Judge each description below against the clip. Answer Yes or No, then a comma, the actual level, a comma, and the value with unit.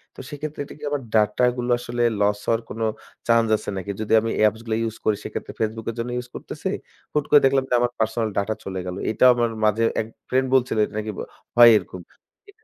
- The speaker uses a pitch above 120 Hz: No, low, 115 Hz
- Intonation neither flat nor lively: No, narrow, 2.2 semitones